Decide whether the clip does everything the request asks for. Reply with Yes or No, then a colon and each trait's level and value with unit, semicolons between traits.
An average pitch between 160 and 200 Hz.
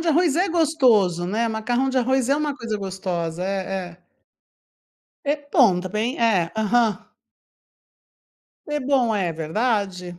No: high, 220 Hz